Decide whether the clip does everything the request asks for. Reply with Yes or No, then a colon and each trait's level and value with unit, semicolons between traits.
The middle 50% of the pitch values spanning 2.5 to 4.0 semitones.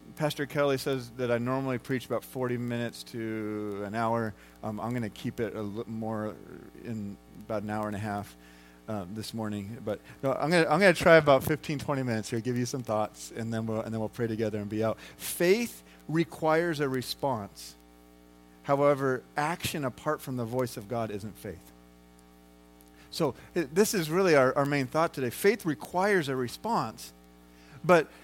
No: average, 5.2 semitones